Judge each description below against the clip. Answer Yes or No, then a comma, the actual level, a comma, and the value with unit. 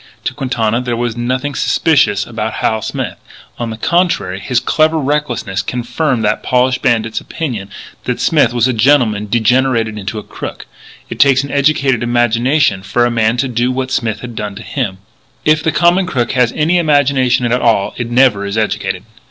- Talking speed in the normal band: Yes, average, 180 wpm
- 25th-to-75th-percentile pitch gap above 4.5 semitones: No, average, 3.5 semitones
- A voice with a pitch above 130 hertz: No, low, 120 Hz